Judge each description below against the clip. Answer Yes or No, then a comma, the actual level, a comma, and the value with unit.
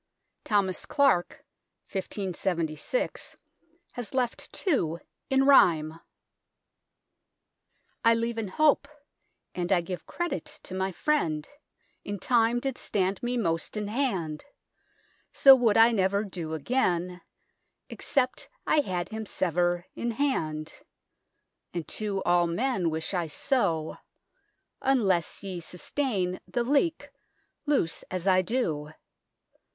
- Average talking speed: No, slow, 115 wpm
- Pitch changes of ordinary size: No, wide, 6.0 semitones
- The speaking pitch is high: Yes, high, 195 Hz